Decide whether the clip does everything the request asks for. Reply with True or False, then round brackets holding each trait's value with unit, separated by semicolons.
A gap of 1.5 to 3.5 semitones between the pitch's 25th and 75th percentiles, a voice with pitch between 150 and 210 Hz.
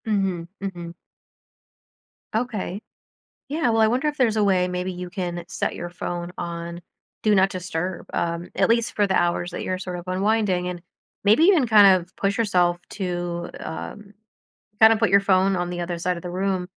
True (3.0 semitones; 185 Hz)